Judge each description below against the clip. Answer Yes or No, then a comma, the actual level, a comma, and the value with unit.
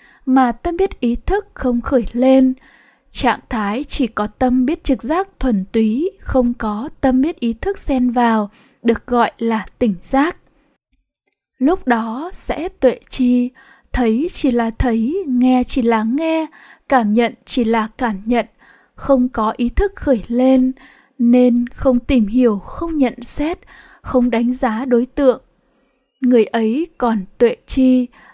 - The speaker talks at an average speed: No, slow, 155 wpm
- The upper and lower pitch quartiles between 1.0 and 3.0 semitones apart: Yes, narrow, 2.5 semitones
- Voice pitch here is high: Yes, very high, 255 Hz